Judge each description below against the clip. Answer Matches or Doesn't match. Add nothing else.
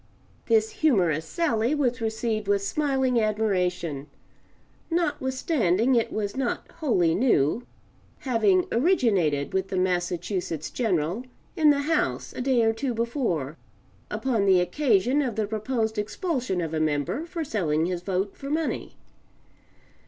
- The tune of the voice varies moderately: Doesn't match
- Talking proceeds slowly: Matches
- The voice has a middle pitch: Doesn't match